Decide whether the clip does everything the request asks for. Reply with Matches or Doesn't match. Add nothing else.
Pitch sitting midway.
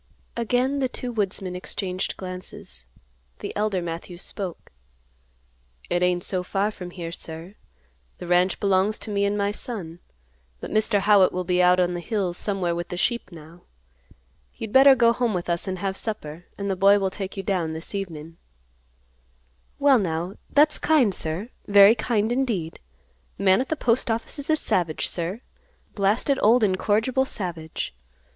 Doesn't match